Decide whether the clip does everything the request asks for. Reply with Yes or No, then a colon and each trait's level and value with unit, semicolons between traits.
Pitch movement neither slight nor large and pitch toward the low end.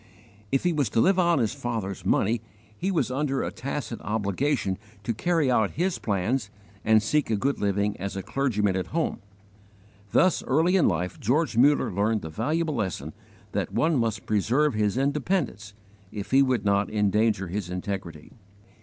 No: wide, 6.0 semitones; low, 115 Hz